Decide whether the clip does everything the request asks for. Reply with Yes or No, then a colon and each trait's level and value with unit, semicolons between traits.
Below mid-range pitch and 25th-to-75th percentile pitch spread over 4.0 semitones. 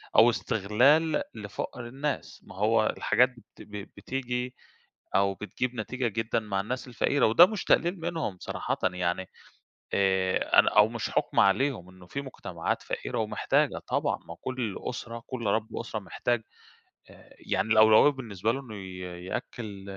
Yes: low, 115 Hz; average, 4.4 semitones